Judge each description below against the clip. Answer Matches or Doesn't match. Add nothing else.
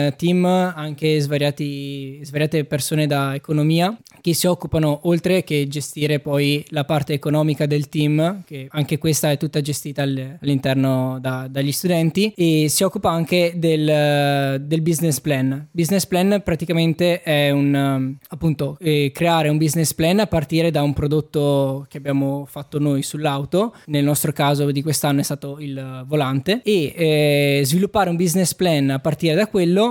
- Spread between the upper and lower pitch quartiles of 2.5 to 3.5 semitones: Matches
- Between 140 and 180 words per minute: Matches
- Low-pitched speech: Doesn't match